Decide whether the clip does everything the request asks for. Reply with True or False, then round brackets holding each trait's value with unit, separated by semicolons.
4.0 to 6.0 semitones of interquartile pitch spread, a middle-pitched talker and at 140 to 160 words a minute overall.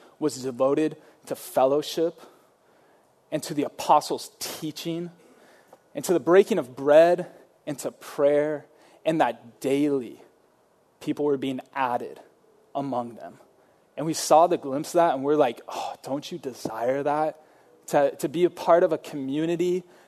False (3.3 semitones; 150 Hz; 150 wpm)